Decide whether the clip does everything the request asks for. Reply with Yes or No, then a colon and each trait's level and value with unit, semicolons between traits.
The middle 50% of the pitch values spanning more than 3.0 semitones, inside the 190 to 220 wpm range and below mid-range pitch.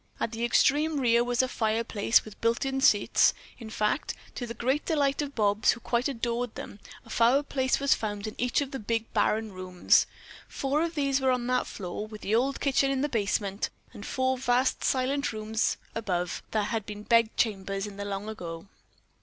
No: average, 3.9 semitones; average, 195 wpm; high, 230 Hz